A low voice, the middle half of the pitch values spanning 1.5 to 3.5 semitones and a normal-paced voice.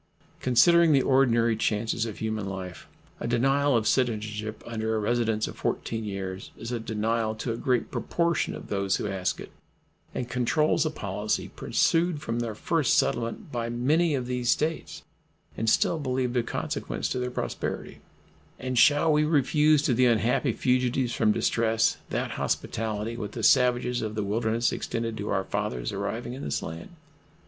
Yes: low, 120 Hz; average, 3.0 semitones; average, 170 wpm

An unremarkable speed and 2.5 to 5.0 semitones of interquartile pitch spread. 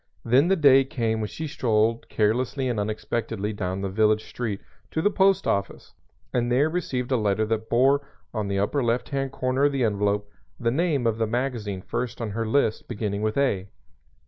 Yes: average, 195 wpm; average, 4.0 semitones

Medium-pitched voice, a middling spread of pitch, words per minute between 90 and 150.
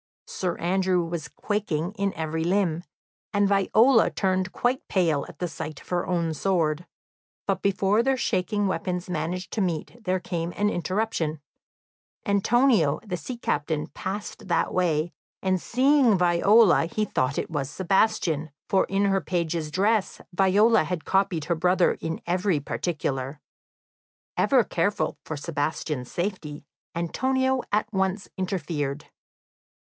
Yes: medium, 180 Hz; average, 3.8 semitones; slow, 135 wpm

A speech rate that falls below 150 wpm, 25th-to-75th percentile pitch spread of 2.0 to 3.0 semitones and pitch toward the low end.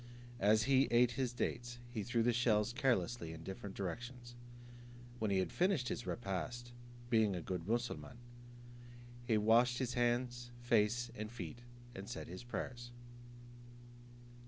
Yes: average, 140 wpm; narrow, 2.6 semitones; low, 120 Hz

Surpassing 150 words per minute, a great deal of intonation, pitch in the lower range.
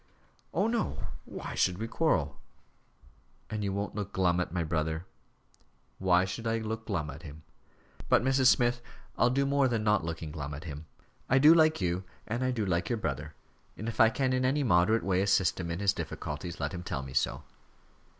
Yes: average, 200 wpm; wide, 6.5 semitones; low, 100 Hz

